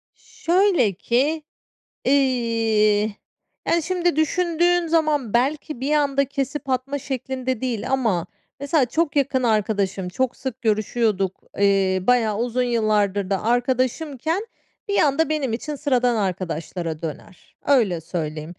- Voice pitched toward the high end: Yes, very high, 250 Hz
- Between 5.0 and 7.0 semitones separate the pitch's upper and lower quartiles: Yes, wide, 5.6 semitones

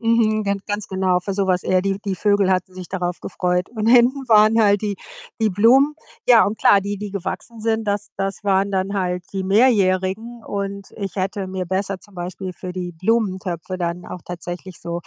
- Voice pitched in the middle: No, high, 195 Hz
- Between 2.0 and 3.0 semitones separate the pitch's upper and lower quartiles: Yes, narrow, 2.4 semitones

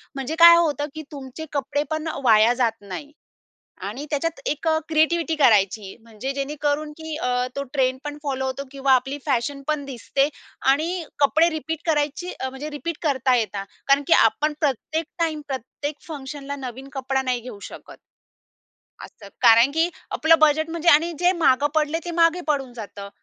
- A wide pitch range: No, average, 3.3 semitones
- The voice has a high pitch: Yes, very high, 285 Hz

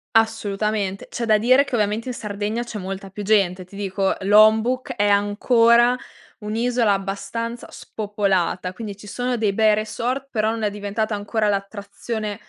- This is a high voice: Yes, high, 215 Hz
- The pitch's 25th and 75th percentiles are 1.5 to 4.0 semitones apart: Yes, narrow, 2.4 semitones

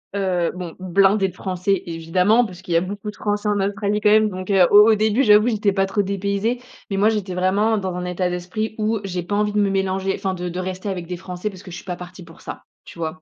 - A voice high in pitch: Yes, high, 195 Hz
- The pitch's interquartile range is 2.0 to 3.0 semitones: Yes, narrow, 2.5 semitones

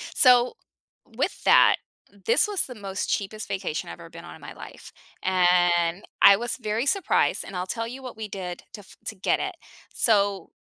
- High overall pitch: Yes, high, 205 Hz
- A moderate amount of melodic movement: Yes, average, 4.5 semitones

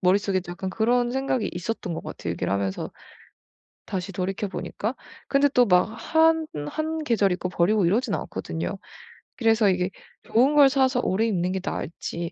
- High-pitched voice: Yes, high, 205 Hz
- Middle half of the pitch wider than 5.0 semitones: Yes, wide, 5.5 semitones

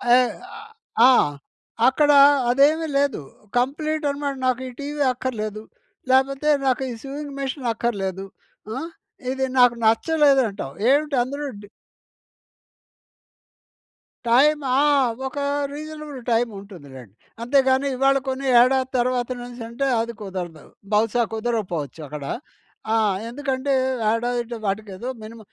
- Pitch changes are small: No, average, 3.7 semitones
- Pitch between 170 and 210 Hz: No, very high, 255 Hz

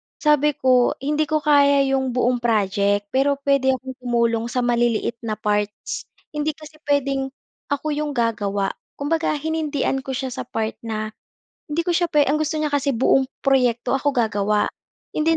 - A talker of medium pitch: No, very high, 270 Hz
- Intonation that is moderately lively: Yes, average, 4.1 semitones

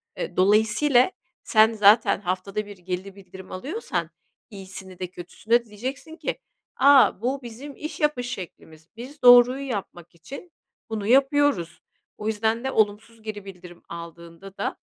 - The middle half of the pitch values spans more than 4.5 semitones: Yes, average, 5.3 semitones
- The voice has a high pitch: Yes, high, 215 Hz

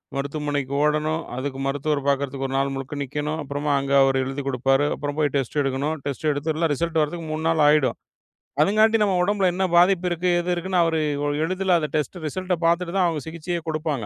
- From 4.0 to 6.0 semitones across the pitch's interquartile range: No, average, 3.4 semitones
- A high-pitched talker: No, medium, 150 Hz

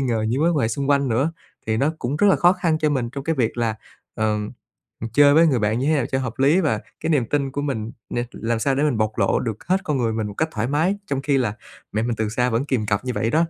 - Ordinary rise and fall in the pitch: Yes, average, 4.6 semitones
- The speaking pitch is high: No, low, 130 Hz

